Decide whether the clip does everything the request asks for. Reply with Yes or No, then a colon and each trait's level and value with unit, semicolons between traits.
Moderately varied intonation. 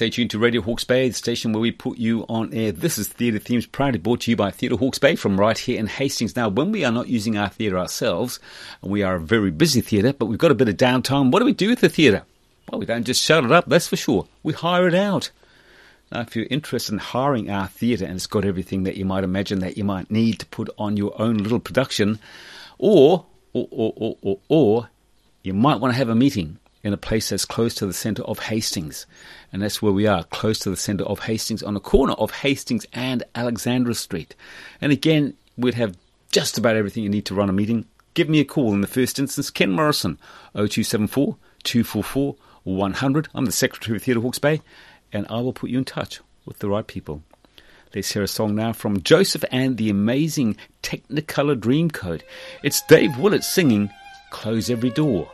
Yes: average, 4.0 semitones